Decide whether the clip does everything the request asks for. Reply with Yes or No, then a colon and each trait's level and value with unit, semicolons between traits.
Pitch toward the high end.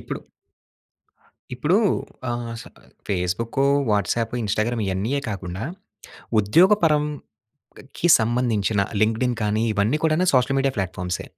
No: low, 115 Hz